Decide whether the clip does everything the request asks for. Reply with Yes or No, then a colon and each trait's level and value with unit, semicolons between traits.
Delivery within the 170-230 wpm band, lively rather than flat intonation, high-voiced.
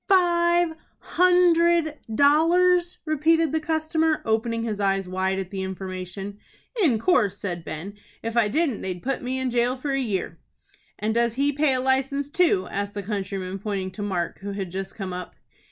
Yes: average, 175 wpm; wide, 8.3 semitones; high, 235 Hz